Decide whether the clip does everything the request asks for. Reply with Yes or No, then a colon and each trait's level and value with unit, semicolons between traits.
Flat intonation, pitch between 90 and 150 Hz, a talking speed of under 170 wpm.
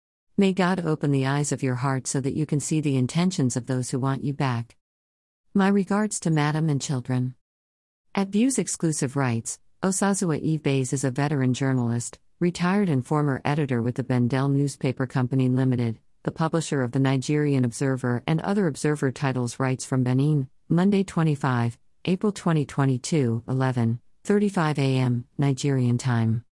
No: average, 3.7 semitones; medium, 140 Hz; average, 155 wpm